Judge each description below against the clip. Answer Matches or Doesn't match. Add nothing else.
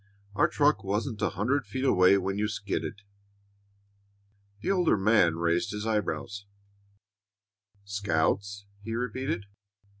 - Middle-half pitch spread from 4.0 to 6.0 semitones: Doesn't match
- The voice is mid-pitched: Doesn't match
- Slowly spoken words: Matches